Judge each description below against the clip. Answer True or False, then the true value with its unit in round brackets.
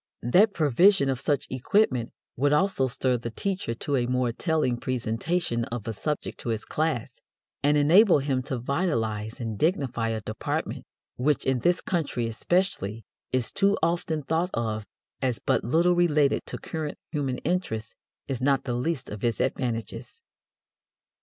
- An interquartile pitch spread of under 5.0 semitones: False (5.4 semitones)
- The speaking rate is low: False (155 wpm)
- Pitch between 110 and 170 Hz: True (135 Hz)